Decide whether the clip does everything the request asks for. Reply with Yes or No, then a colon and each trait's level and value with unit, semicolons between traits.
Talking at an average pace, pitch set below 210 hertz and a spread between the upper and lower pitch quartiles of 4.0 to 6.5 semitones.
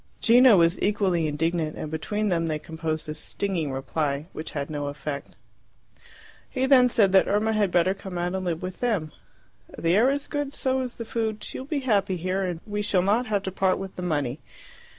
No: fast, 210 wpm; medium, 185 Hz; average, 5.2 semitones